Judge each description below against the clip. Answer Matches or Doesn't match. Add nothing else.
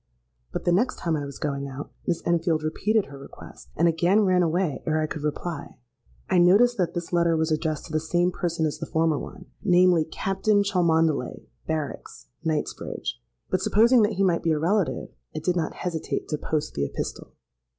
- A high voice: Doesn't match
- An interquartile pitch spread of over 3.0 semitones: Doesn't match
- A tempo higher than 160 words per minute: Matches